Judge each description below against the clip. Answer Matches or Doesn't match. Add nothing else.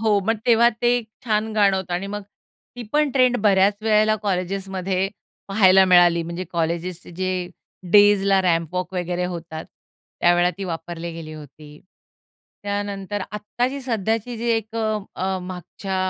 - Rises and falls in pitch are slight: Doesn't match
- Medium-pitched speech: Doesn't match